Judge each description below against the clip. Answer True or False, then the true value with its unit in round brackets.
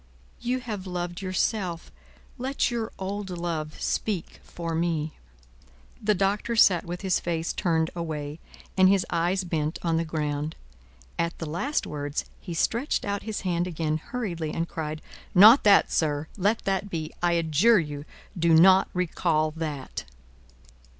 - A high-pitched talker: False (175 Hz)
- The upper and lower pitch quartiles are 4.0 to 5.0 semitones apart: False (3.6 semitones)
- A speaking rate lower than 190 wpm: True (150 wpm)